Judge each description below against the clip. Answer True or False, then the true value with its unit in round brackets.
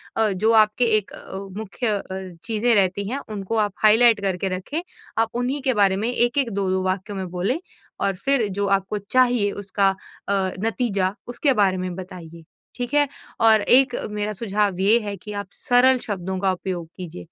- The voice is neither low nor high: False (205 Hz)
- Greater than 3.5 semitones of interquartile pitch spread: True (3.9 semitones)